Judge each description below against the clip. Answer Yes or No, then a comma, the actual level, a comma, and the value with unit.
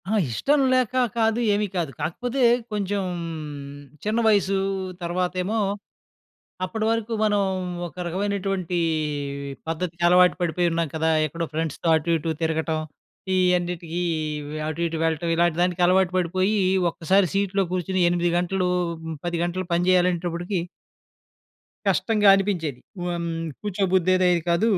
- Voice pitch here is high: No, medium, 180 Hz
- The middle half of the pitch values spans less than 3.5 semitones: Yes, narrow, 2.6 semitones